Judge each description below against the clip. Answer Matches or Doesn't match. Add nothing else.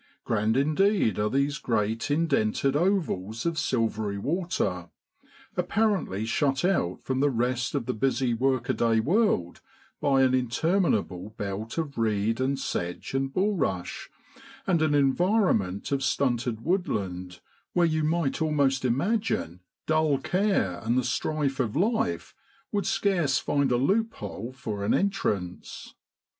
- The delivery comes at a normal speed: Doesn't match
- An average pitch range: Doesn't match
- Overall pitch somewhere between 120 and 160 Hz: Matches